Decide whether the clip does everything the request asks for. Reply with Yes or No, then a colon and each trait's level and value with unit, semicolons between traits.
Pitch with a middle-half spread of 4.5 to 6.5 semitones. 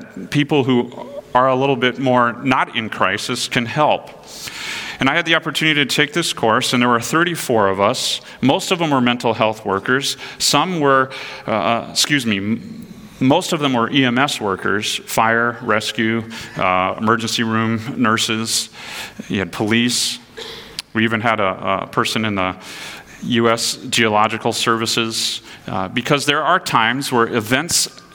No: average, 3.7 semitones